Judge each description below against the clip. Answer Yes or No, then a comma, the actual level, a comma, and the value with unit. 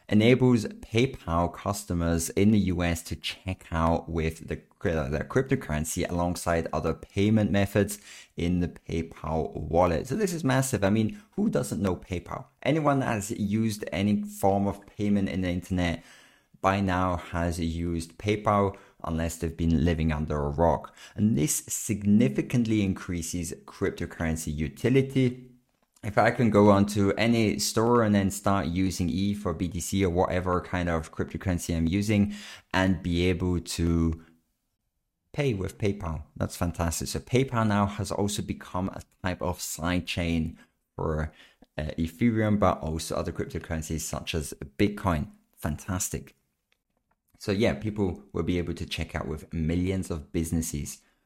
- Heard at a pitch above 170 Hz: No, very low, 90 Hz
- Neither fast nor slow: Yes, average, 145 wpm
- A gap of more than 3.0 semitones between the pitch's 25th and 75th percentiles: Yes, average, 3.8 semitones